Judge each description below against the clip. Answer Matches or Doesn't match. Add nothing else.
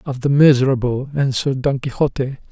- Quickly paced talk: Doesn't match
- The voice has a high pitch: Doesn't match